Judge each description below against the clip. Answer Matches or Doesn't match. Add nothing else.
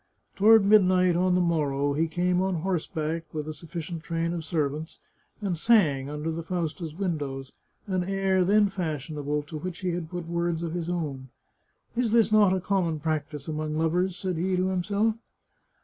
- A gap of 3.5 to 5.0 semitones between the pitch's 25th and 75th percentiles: Doesn't match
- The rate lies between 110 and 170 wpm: Doesn't match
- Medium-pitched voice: Matches